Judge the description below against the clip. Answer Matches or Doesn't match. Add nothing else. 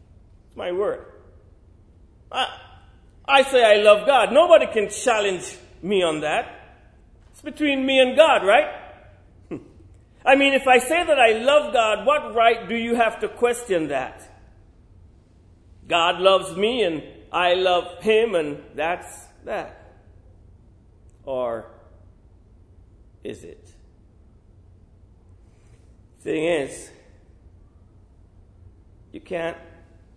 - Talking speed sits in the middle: Doesn't match